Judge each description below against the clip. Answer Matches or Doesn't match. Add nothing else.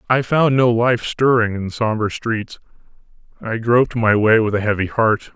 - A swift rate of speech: Doesn't match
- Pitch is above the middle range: Doesn't match